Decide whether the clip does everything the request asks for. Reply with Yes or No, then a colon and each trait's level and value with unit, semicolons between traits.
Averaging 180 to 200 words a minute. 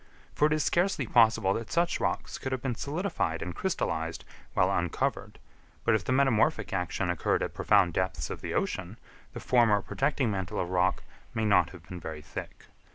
Yes: average, 185 wpm